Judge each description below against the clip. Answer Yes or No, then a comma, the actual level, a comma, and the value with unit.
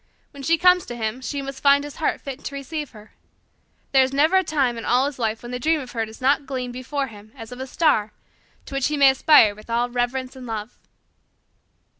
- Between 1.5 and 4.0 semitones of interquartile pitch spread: Yes, average, 2.9 semitones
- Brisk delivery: Yes, fast, 235 wpm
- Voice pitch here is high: Yes, very high, 260 Hz